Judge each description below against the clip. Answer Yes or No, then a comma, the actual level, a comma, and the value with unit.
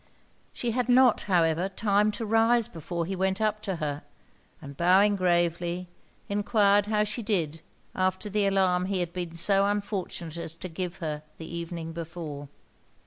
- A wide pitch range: No, average, 3.5 semitones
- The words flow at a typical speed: Yes, average, 160 wpm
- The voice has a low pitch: No, medium, 185 Hz